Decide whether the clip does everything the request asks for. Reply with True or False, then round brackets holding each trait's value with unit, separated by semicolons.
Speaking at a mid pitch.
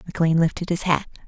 True (165 Hz)